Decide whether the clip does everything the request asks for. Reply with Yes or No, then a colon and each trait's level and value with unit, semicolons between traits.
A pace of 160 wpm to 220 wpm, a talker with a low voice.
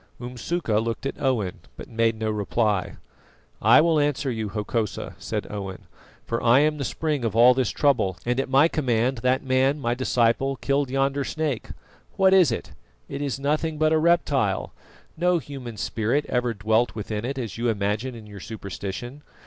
Yes: average, 175 wpm; low, 125 Hz